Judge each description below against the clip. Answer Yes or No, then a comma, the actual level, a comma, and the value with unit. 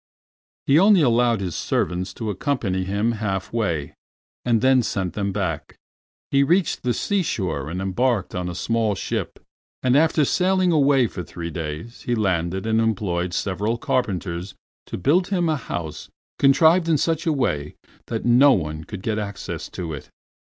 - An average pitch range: No, wide, 7.1 semitones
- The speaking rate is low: No, average, 165 wpm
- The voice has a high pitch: No, low, 110 Hz